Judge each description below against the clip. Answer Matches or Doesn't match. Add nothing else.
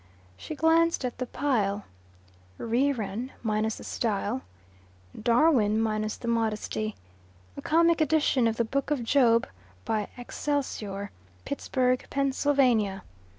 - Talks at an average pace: Doesn't match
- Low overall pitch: Doesn't match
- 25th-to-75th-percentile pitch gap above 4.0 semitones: Matches